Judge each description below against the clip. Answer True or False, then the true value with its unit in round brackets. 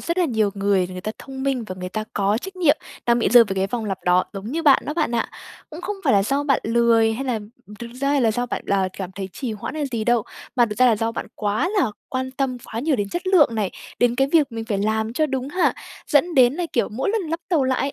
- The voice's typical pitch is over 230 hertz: True (240 Hz)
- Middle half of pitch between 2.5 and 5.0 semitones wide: True (4.7 semitones)